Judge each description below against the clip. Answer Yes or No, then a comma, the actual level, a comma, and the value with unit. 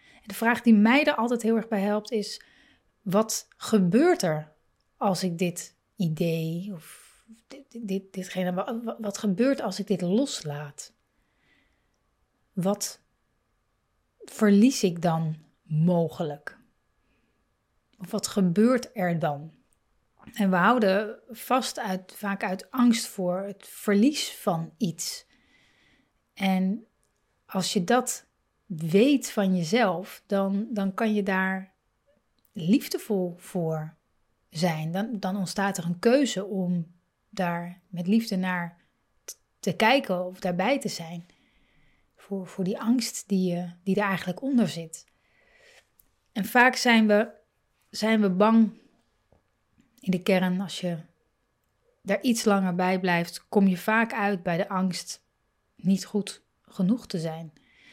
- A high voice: Yes, high, 200 Hz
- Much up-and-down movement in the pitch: No, average, 3.8 semitones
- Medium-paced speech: No, slow, 125 wpm